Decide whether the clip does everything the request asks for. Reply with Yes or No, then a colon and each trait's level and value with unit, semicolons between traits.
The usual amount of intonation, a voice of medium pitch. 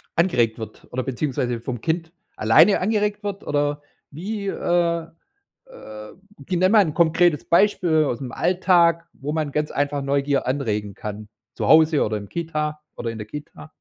No: wide, 5.7 semitones; medium, 150 Hz